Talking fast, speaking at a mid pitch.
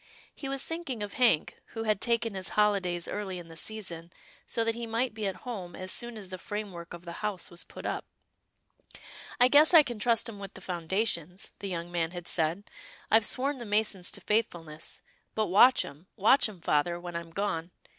No: fast, 215 wpm; high, 200 Hz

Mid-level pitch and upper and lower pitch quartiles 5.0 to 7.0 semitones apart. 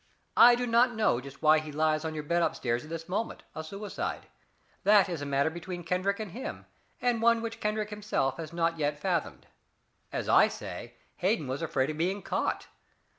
Yes: medium, 170 Hz; wide, 5.4 semitones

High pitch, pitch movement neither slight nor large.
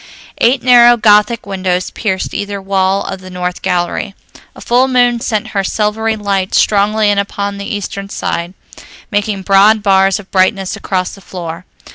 No: high, 200 Hz; narrow, 2.1 semitones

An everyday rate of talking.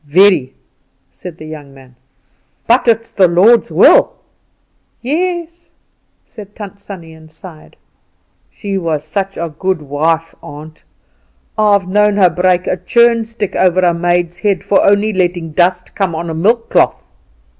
Yes: average, 145 wpm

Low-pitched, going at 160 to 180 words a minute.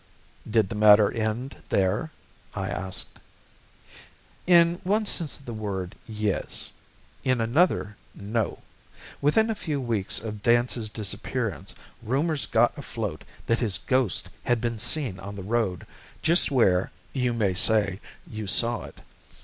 No: low, 115 Hz; slow, 135 wpm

